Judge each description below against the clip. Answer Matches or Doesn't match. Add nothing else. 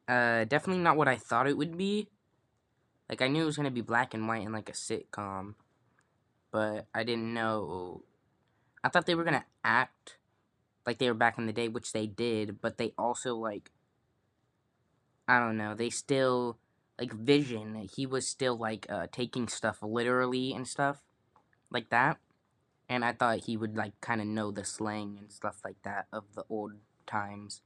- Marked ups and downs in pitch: Doesn't match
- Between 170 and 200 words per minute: Matches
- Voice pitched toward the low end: Matches